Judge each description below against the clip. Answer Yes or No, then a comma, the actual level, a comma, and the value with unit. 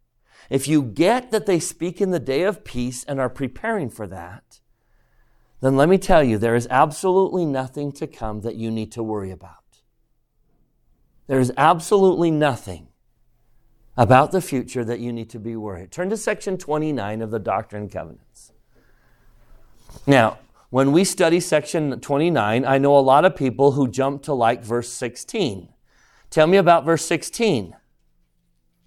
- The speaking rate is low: No, average, 160 wpm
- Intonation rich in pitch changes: Yes, wide, 5.9 semitones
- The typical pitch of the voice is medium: No, low, 130 Hz